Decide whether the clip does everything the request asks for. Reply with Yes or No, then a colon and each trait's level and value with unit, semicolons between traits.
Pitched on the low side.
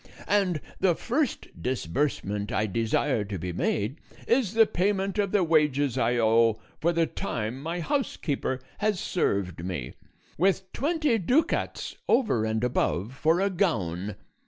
No: medium, 150 Hz